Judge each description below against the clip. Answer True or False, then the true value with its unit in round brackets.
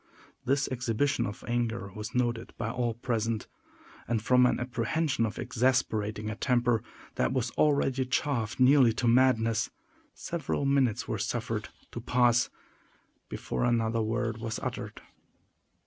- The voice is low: True (120 Hz)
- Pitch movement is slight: True (2.3 semitones)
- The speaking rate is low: True (130 wpm)